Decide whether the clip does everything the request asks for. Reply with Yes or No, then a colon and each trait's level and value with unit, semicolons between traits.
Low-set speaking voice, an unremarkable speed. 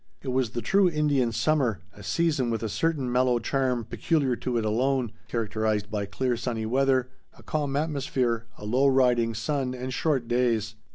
Yes: low, 125 Hz; average, 175 wpm